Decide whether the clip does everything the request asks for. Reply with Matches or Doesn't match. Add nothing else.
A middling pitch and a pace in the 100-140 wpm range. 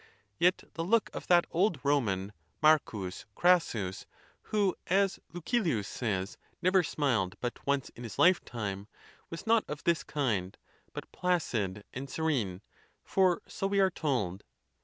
Matches